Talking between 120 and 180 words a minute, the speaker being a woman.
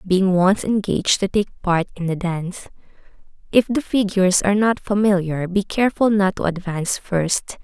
Yes: average, 165 wpm; female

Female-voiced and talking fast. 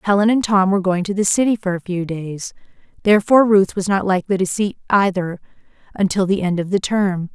Yes: female; fast, 210 wpm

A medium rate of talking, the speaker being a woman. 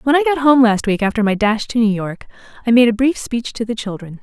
No: fast, 285 wpm; female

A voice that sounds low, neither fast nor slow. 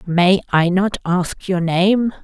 No: medium, 185 Hz; average, 160 wpm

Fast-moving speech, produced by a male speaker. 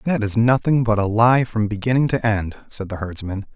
Yes: fast, 220 wpm; male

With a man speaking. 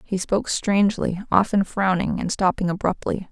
No: female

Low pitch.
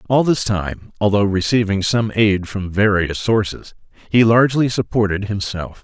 Yes: low, 105 Hz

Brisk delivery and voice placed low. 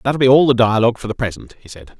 Yes: fast, 300 wpm; low, 120 Hz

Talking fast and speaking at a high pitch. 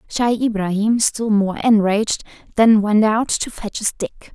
No: average, 165 wpm; high, 215 Hz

